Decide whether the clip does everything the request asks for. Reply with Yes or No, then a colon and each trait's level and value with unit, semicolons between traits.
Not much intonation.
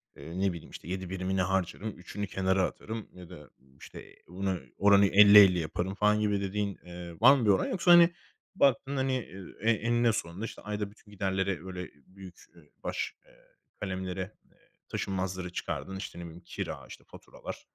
Yes: narrow, 2.3 semitones